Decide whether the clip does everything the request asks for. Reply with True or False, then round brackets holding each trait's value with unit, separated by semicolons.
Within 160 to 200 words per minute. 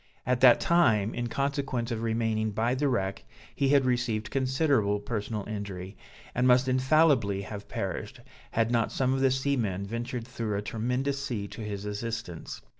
True (165 wpm)